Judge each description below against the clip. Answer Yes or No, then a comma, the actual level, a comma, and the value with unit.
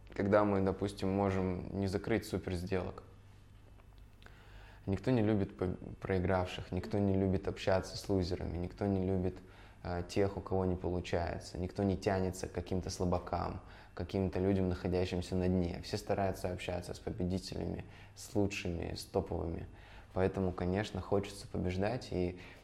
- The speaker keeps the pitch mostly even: Yes, narrow, 1.7 semitones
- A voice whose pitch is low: Yes, very low, 95 Hz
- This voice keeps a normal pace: Yes, average, 140 wpm